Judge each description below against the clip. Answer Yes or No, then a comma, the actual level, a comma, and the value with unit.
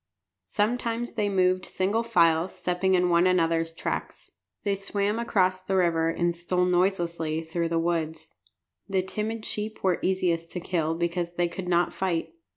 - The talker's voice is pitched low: No, medium, 180 Hz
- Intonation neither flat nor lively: No, narrow, 2.3 semitones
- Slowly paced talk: No, average, 160 wpm